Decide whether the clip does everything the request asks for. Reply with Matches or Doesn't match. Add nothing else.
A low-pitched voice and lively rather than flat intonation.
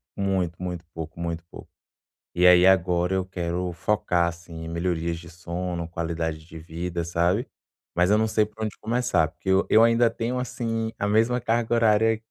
Doesn't match